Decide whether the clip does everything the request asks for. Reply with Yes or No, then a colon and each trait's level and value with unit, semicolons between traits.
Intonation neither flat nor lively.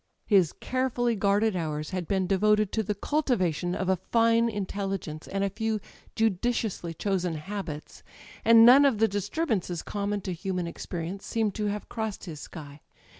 Yes: average, 3.7 semitones